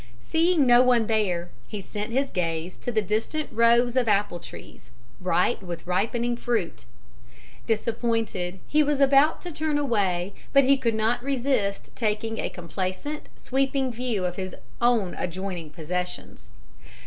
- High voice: Yes, high, 225 Hz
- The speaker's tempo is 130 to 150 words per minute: Yes, average, 145 wpm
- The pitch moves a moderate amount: No, wide, 5.7 semitones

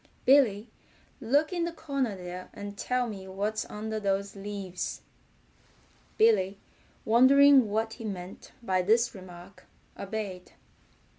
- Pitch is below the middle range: No, high, 210 Hz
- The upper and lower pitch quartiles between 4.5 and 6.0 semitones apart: No, average, 3.8 semitones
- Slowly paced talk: Yes, slow, 120 wpm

